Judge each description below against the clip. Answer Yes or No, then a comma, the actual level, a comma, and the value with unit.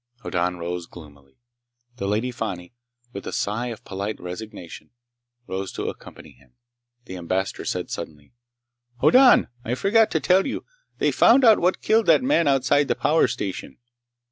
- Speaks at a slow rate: No, average, 155 wpm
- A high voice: No, low, 105 Hz